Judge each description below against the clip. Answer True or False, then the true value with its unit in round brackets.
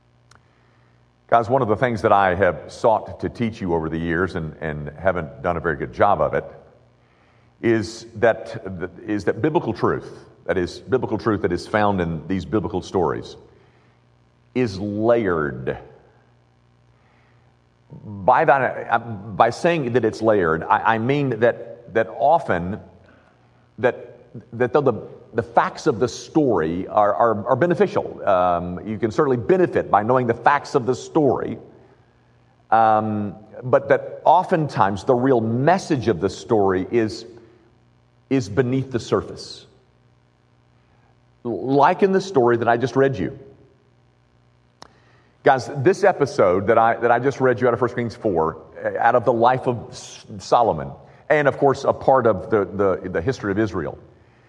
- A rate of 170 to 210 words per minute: False (155 wpm)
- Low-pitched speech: True (110 Hz)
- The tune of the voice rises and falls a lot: True (7.6 semitones)